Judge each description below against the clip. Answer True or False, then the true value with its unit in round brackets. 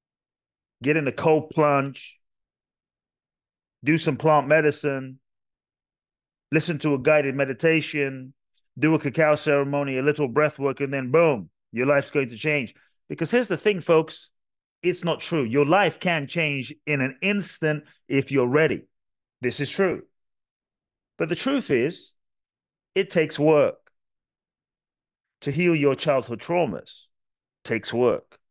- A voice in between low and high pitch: True (150 Hz)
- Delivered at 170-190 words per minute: False (135 wpm)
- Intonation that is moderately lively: True (3.0 semitones)